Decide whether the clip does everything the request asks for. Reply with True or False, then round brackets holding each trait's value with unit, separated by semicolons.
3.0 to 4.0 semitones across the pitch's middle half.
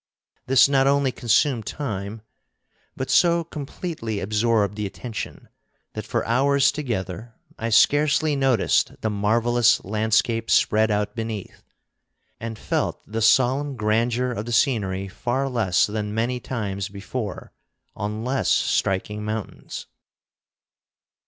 True (3.6 semitones)